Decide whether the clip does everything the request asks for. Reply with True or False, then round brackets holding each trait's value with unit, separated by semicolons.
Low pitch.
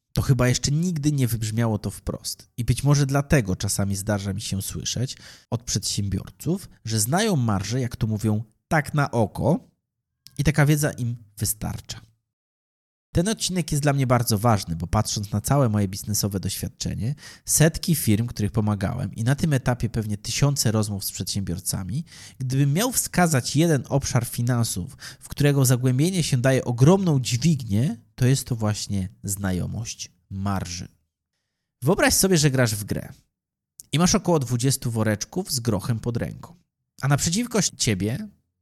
True (120 Hz)